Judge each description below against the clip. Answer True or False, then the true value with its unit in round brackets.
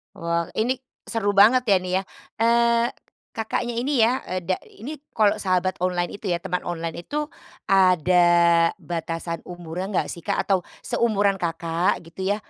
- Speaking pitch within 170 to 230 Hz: True (185 Hz)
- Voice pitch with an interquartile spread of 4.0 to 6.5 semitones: True (4.4 semitones)